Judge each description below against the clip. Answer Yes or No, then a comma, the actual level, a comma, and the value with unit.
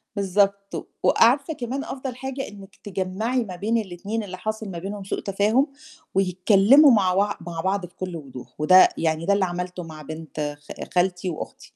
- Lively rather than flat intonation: No, average, 3.4 semitones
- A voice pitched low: No, high, 195 Hz